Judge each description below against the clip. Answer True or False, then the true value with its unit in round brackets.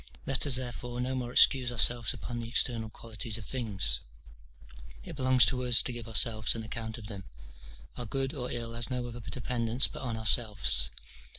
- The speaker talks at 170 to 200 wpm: True (185 wpm)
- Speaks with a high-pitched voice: False (120 Hz)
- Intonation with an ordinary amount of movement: False (2.1 semitones)